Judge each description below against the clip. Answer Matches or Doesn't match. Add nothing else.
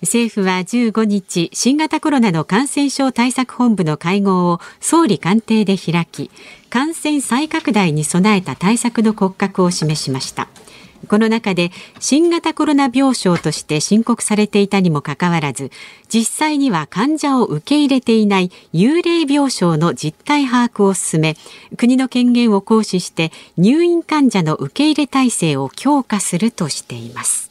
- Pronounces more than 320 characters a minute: Doesn't match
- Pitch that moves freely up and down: Matches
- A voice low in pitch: Doesn't match